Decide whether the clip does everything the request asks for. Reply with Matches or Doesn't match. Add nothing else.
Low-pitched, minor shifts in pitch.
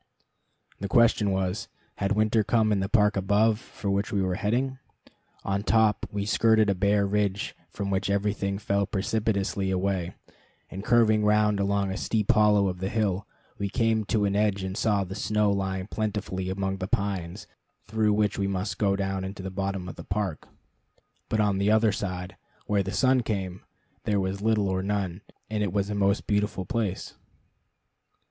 Matches